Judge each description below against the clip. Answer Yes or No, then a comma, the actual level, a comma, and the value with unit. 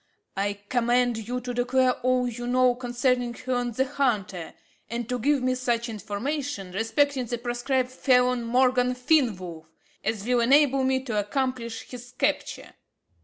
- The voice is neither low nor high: No, high, 245 Hz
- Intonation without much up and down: Yes, narrow, 1.7 semitones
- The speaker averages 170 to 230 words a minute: No, average, 145 wpm